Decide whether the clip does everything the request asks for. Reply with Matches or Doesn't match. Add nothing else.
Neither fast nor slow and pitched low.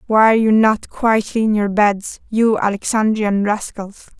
Doesn't match